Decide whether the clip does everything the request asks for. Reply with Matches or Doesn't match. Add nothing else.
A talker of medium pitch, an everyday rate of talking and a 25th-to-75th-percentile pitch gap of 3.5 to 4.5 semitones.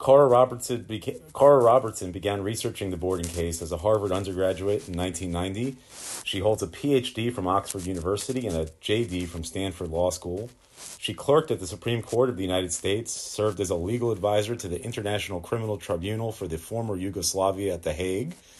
Doesn't match